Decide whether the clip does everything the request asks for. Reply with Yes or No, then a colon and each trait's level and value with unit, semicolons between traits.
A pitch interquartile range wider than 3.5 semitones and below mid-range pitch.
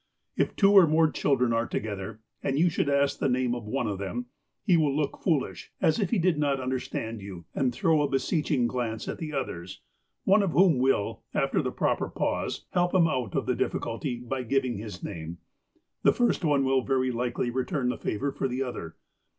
Yes: average, 4.3 semitones; low, 130 Hz